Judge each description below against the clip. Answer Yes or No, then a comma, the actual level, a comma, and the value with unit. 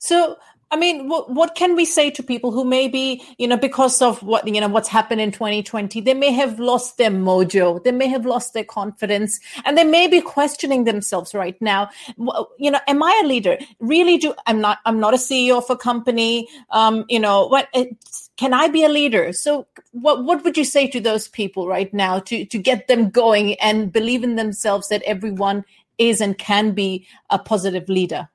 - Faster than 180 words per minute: Yes, fast, 205 wpm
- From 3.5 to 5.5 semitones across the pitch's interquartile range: Yes, average, 4.3 semitones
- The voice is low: No, high, 235 Hz